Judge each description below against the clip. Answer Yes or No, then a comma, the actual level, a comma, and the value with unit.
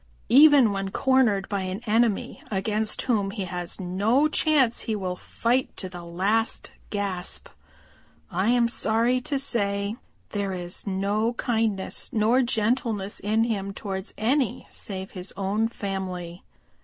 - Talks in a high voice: Yes, high, 210 Hz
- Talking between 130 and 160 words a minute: Yes, average, 140 wpm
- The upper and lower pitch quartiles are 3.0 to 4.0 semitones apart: Yes, average, 3.3 semitones